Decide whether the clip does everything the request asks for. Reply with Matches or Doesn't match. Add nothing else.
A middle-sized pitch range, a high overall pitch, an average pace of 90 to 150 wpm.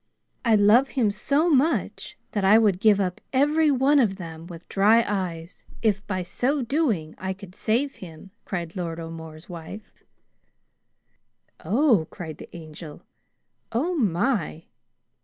Doesn't match